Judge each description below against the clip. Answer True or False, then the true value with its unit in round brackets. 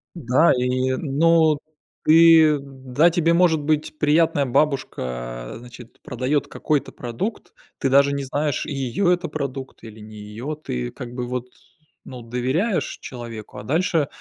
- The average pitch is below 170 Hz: True (135 Hz)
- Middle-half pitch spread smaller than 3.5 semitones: False (4.2 semitones)